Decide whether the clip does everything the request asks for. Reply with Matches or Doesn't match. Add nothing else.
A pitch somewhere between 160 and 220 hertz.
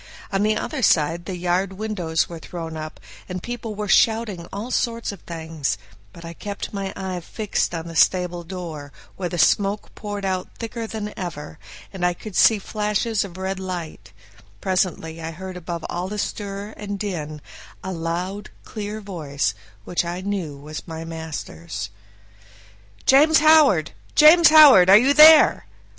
Matches